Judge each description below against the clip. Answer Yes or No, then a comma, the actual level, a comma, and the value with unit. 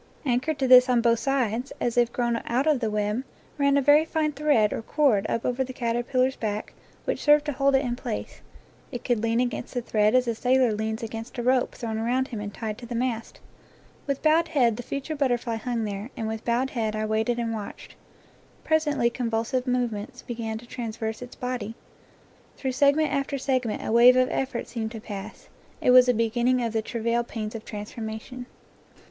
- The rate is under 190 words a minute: No, fast, 205 wpm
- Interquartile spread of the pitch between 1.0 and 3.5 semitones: Yes, average, 2.7 semitones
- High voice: Yes, high, 240 Hz